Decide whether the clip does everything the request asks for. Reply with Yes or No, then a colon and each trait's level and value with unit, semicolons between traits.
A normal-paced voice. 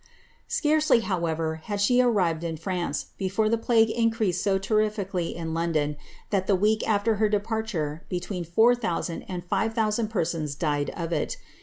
Yes: average, 160 wpm